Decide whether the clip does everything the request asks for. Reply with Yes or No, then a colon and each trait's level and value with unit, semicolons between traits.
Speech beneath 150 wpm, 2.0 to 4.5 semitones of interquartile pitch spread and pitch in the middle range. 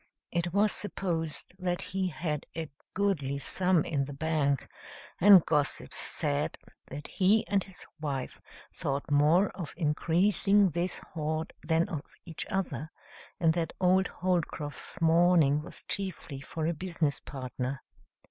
Yes: slow, 135 wpm; average, 3.9 semitones; medium, 165 Hz